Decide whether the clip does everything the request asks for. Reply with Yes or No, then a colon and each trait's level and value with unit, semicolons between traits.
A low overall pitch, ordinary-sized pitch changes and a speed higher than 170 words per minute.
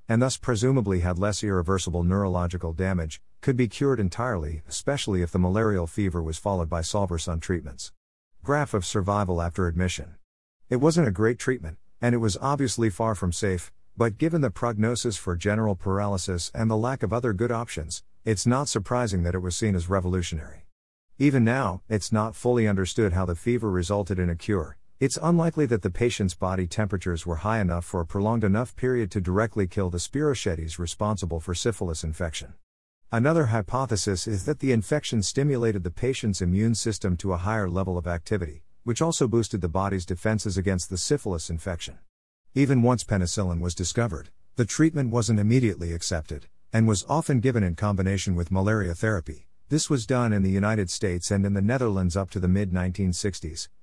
Yes: low, 100 Hz; average, 4.6 semitones; average, 180 wpm